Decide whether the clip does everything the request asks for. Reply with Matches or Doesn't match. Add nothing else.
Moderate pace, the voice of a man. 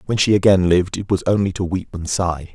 Doesn't match